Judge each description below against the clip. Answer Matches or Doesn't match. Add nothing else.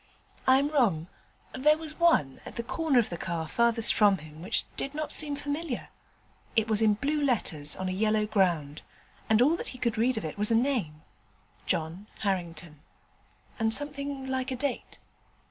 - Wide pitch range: Matches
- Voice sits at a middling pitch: Doesn't match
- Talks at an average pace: Matches